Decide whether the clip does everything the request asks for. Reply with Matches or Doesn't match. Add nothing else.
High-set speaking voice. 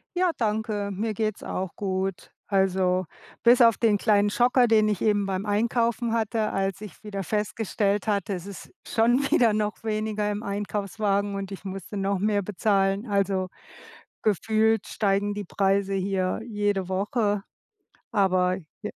Matches